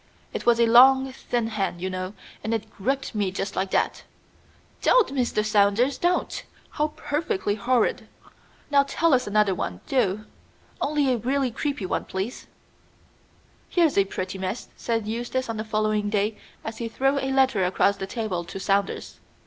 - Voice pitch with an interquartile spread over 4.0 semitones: Yes, average, 4.8 semitones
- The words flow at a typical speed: Yes, average, 165 wpm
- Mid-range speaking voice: No, high, 225 Hz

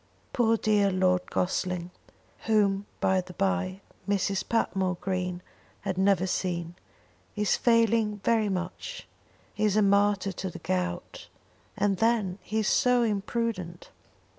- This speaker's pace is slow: Yes, slow, 130 wpm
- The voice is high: Yes, high, 195 Hz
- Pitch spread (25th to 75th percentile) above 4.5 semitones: No, average, 2.7 semitones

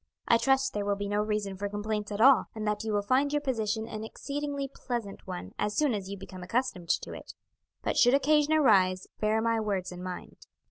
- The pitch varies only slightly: No, average, 4.5 semitones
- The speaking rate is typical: No, fast, 220 wpm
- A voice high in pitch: Yes, high, 215 Hz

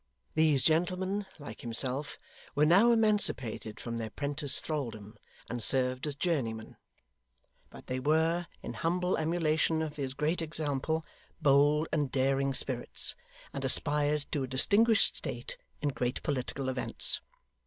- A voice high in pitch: No, medium, 145 Hz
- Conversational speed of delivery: No, slow, 130 wpm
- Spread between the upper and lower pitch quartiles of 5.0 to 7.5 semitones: No, average, 3.8 semitones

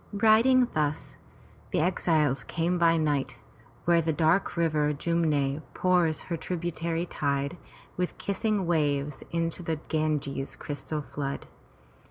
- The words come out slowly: Yes, slow, 120 wpm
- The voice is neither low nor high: Yes, medium, 160 Hz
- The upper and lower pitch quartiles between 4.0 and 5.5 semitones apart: No, average, 2.8 semitones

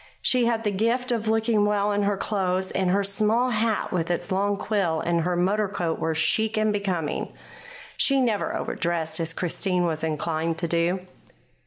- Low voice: No, high, 195 Hz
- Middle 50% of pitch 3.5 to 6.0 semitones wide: Yes, average, 4.0 semitones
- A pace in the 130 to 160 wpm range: No, average, 180 wpm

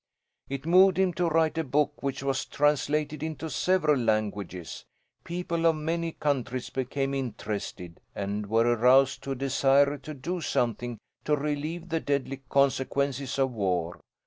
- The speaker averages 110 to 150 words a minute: Yes, average, 145 wpm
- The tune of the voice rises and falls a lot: No, average, 3.7 semitones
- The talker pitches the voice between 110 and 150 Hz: Yes, medium, 140 Hz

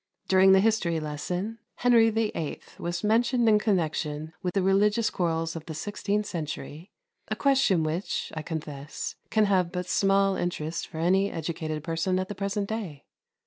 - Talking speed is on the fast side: No, average, 160 wpm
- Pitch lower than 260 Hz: Yes, medium, 185 Hz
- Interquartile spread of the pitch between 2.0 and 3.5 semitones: No, average, 4.3 semitones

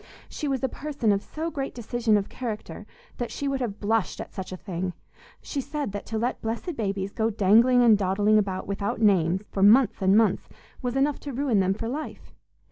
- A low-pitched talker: No, high, 220 Hz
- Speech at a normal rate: No, fast, 210 wpm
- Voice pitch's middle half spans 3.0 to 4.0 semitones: No, average, 4.4 semitones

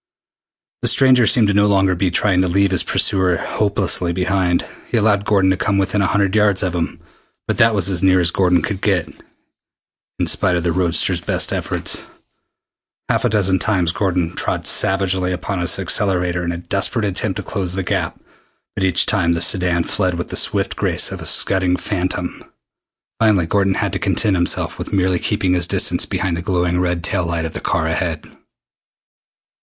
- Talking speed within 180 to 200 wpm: Yes, average, 190 wpm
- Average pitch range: No, narrow, 2.1 semitones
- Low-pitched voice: Yes, very low, 95 Hz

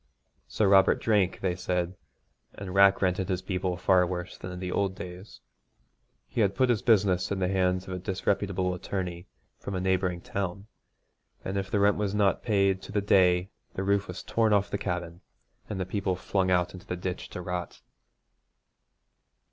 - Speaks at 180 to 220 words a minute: Yes, average, 185 wpm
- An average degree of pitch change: No, narrow, 1.7 semitones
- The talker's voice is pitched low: Yes, very low, 95 Hz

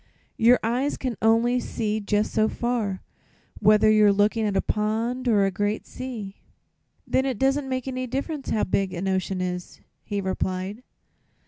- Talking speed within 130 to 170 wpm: Yes, average, 160 wpm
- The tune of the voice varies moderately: Yes, average, 3.8 semitones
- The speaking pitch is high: Yes, high, 215 Hz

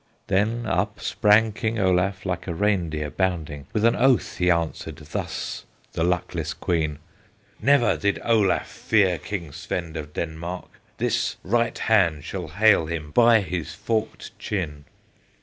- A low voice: Yes, very low, 90 Hz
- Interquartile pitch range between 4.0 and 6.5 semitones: Yes, average, 4.6 semitones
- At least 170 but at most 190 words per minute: No, average, 145 wpm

